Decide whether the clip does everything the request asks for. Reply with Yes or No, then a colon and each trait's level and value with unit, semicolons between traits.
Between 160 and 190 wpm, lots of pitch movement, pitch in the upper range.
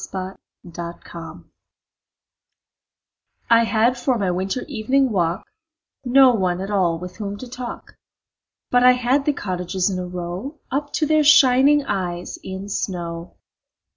No: average, 140 wpm; wide, 5.9 semitones; high, 205 Hz